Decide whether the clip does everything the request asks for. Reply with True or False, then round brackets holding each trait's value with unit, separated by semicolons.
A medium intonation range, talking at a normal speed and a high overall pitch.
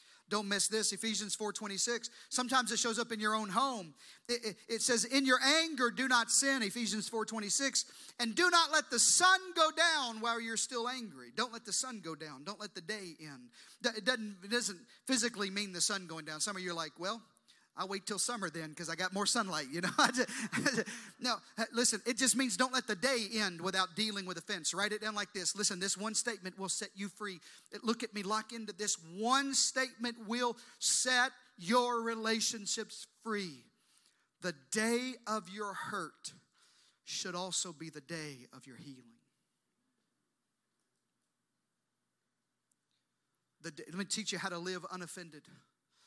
True (4.3 semitones; 185 wpm; 215 Hz)